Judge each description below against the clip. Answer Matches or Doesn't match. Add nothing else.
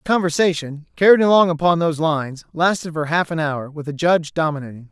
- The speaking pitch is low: Doesn't match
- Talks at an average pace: Matches